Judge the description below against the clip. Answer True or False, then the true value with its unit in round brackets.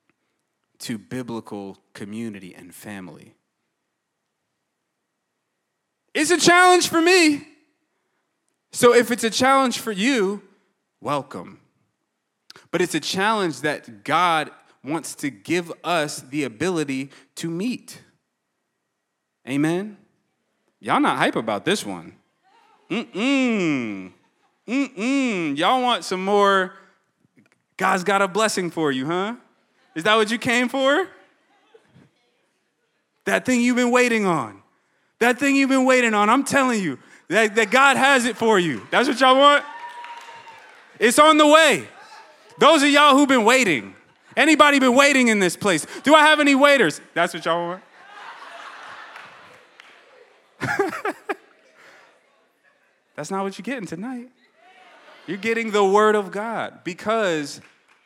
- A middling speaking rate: False (130 wpm)